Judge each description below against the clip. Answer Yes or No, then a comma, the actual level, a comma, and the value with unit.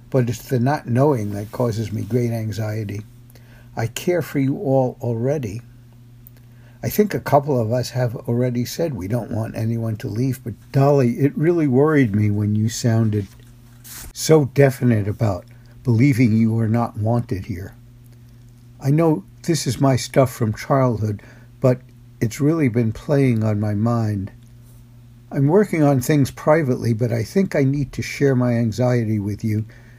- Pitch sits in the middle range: No, low, 120 Hz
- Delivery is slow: No, average, 160 wpm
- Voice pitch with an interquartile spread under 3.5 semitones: Yes, narrow, 2.6 semitones